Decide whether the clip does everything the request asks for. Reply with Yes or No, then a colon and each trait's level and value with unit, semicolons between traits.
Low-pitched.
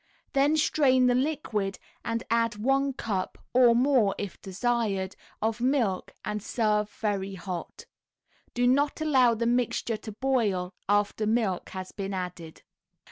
No: high, 225 Hz